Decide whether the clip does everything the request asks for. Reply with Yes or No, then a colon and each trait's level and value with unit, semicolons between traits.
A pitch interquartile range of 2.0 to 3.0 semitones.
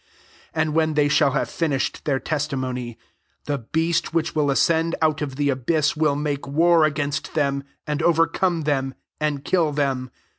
Yes: narrow, 2.5 semitones